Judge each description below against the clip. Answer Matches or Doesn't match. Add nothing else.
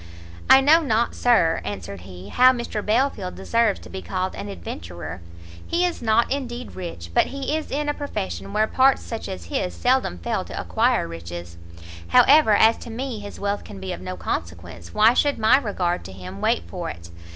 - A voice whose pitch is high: Matches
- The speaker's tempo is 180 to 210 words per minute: Matches